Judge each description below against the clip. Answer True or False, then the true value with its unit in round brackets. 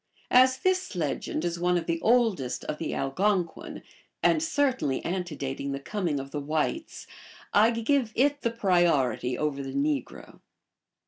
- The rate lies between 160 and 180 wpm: False (150 wpm)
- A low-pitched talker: False (175 Hz)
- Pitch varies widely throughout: True (9.0 semitones)